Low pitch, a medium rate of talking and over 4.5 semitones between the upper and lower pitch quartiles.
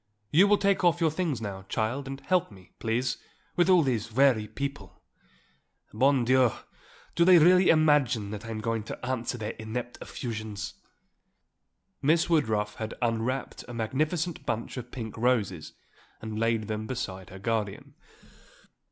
Yes: low, 120 Hz; average, 150 wpm; average, 5.2 semitones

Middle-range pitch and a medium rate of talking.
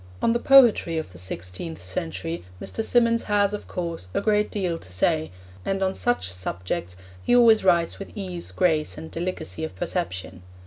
Yes: medium, 170 Hz; average, 175 wpm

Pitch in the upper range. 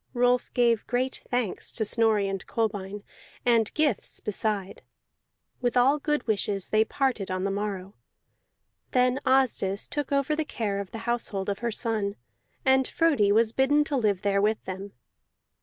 Yes: high, 225 Hz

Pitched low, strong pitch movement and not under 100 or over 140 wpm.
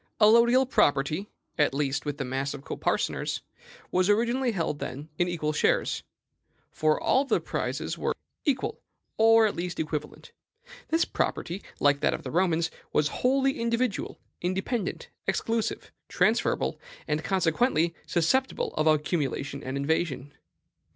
No: medium, 170 Hz; wide, 7.3 semitones; slow, 135 wpm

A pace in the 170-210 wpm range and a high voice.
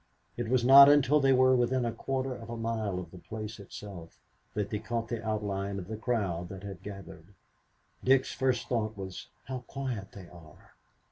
No: average, 190 wpm; low, 110 Hz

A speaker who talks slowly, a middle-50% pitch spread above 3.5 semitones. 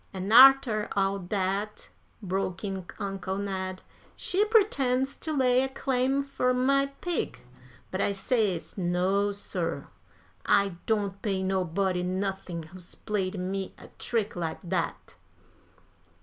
Yes: slow, 125 wpm; average, 5.1 semitones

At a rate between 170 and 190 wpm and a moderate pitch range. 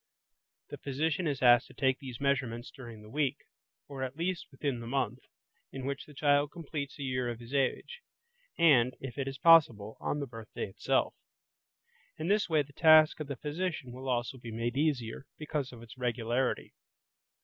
Yes: average, 180 wpm; average, 3.5 semitones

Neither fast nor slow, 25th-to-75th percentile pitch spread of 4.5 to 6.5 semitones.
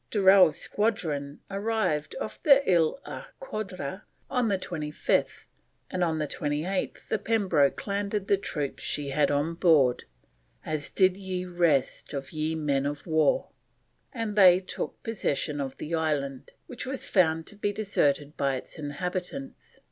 Yes: average, 150 wpm; average, 5.3 semitones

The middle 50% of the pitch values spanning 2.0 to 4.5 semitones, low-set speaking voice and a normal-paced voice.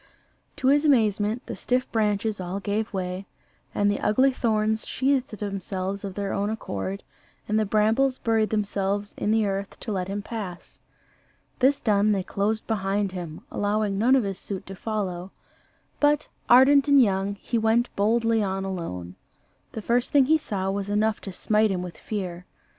No: average, 2.7 semitones; high, 210 Hz; average, 170 wpm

